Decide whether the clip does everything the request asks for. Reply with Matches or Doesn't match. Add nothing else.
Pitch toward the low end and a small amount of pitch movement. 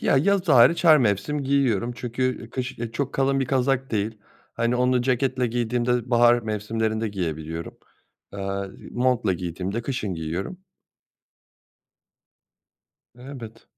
Doesn't match